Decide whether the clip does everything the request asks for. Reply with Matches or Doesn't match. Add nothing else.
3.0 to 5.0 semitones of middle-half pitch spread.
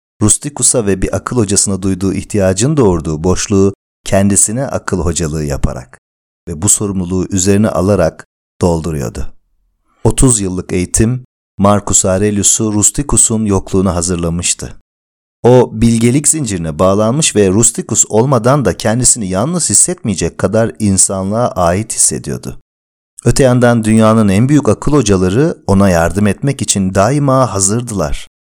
Matches